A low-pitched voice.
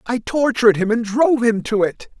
No: high, 230 Hz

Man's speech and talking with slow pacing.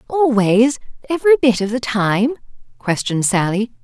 No: female; slow, 125 wpm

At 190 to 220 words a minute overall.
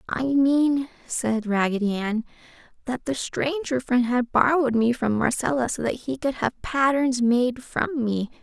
No: average, 165 wpm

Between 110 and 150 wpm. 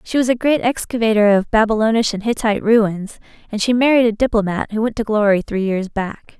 No: fast, 205 wpm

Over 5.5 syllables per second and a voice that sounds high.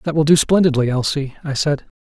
No: 5.9 syllables/s; medium, 145 Hz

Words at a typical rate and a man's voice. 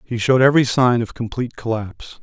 Yes: average, 190 wpm; male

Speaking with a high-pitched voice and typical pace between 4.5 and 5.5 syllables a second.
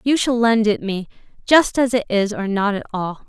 Yes: high, 220 Hz; 5.0 syllables/s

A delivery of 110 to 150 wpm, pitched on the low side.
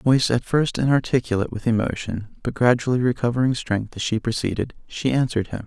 No: average, 190 wpm; low, 120 Hz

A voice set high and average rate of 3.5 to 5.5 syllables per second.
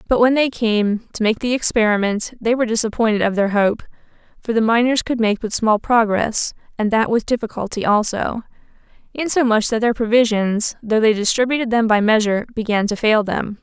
Yes: high, 225 Hz; 5.4 syllables/s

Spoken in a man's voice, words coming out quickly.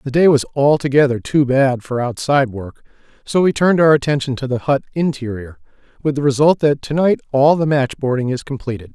No: male; average, 195 wpm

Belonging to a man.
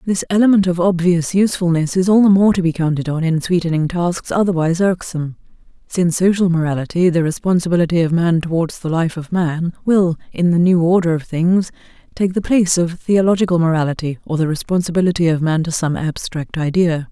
No: female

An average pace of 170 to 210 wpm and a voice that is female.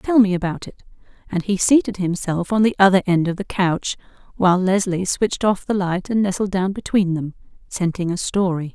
Yes: average, 200 wpm; female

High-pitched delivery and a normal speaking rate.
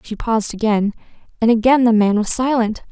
Yes: high, 225 Hz; average, 185 wpm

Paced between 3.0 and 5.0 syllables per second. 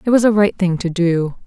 No: 5.5 syllables/s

